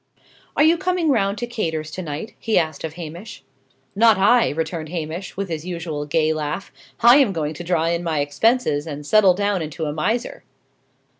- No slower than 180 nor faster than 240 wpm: Yes, average, 190 wpm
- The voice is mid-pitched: Yes, medium, 170 Hz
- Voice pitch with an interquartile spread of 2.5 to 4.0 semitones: No, average, 5.3 semitones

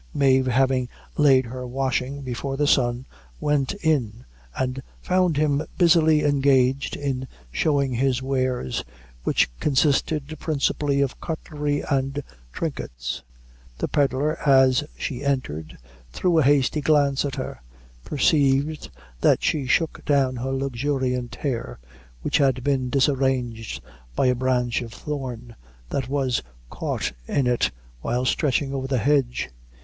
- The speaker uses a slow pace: Yes, slow, 130 wpm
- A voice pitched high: No, low, 135 Hz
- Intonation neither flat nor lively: No, narrow, 2.2 semitones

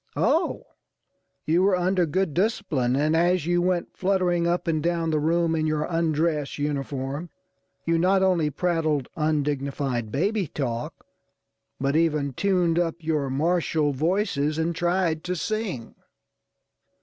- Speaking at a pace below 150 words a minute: Yes, slow, 135 wpm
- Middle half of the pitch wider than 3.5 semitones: No, average, 3.2 semitones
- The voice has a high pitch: No, medium, 165 Hz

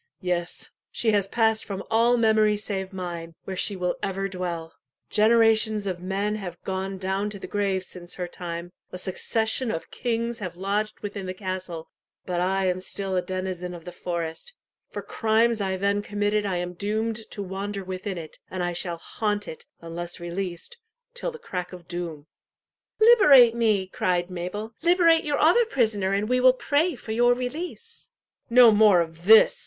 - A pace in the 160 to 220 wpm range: Yes, average, 175 wpm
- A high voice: Yes, high, 195 Hz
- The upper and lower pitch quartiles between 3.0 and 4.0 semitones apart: Yes, average, 3.6 semitones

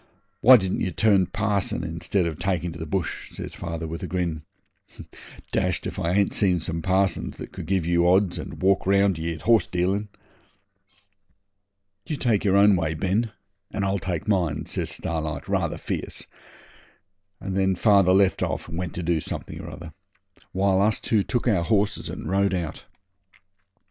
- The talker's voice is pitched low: Yes, very low, 95 Hz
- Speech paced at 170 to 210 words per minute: Yes, average, 175 wpm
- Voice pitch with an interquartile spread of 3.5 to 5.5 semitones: No, average, 2.9 semitones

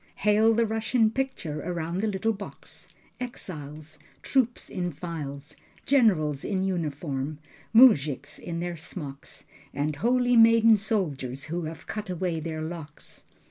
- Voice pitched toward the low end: No, medium, 175 Hz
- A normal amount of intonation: No, wide, 6.5 semitones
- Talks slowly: Yes, slow, 130 wpm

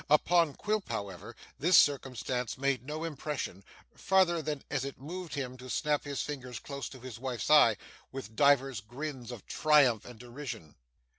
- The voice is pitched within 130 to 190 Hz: Yes, low, 135 Hz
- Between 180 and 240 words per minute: No, average, 160 wpm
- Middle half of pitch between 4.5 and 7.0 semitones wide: No, average, 3.4 semitones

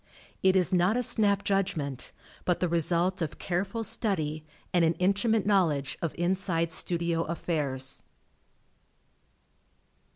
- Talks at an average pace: No, slow, 120 wpm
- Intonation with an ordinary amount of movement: Yes, average, 3.0 semitones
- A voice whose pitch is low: No, medium, 175 Hz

